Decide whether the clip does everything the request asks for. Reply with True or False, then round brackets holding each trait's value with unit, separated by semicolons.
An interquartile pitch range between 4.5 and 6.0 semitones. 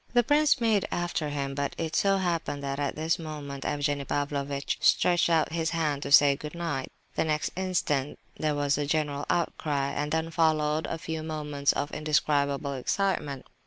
False (2.5 semitones)